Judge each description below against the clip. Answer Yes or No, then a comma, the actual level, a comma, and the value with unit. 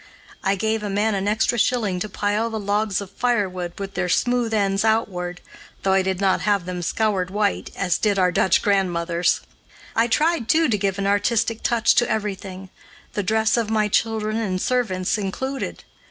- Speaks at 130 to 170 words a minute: No, average, 185 wpm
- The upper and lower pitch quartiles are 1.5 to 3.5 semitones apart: Yes, average, 2.7 semitones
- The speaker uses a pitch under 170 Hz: No, high, 205 Hz